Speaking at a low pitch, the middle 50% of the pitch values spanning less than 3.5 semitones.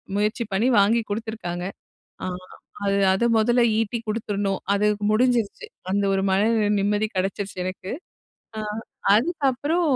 No: high, 215 Hz; average, 3.0 semitones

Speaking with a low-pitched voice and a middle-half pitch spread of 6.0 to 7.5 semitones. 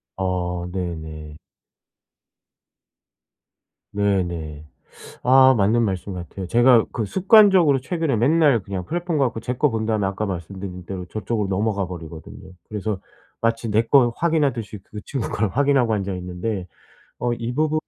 No: low, 105 Hz; wide, 5.4 semitones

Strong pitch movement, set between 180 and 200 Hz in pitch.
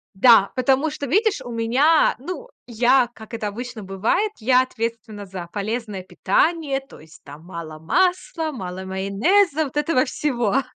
No: wide, 6.7 semitones; high, 240 Hz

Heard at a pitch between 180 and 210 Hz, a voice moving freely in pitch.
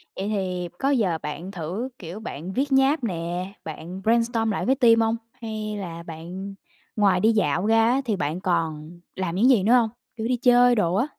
No: high, 200 Hz; average, 4.8 semitones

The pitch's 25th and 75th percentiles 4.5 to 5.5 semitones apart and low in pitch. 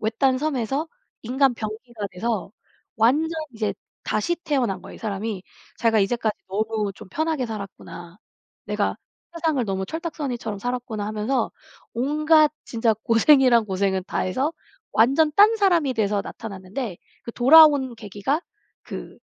No: average, 5.2 semitones; high, 235 Hz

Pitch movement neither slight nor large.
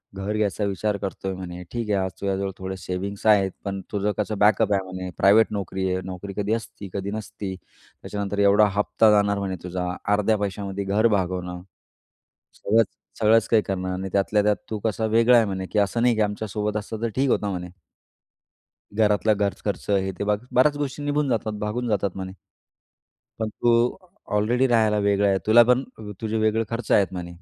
No: narrow, 2.2 semitones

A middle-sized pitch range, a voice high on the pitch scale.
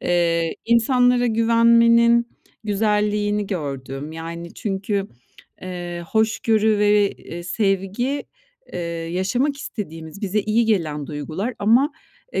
Yes: average, 4.9 semitones; high, 205 Hz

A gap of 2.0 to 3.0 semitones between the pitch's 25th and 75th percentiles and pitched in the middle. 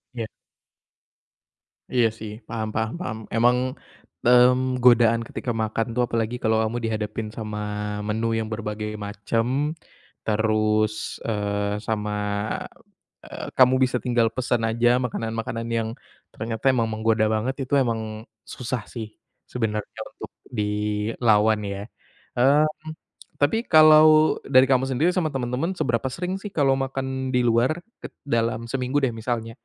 No: narrow, 2.6 semitones; low, 115 Hz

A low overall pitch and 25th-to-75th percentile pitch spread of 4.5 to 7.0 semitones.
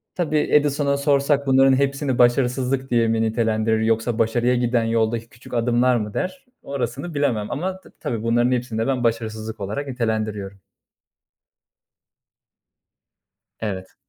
No: low, 120 Hz; average, 3.5 semitones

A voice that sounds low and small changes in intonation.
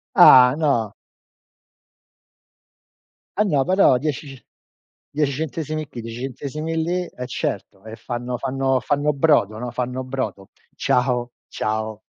No: low, 130 Hz; average, 3.7 semitones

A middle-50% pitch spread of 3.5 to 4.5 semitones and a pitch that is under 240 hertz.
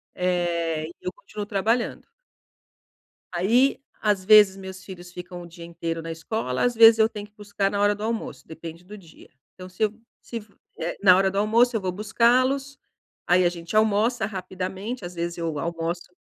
Yes: average, 3.8 semitones; high, 190 Hz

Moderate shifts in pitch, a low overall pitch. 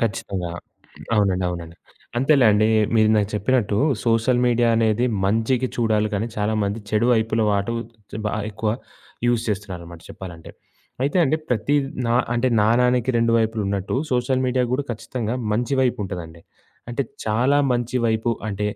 Yes: average, 3.0 semitones; low, 110 Hz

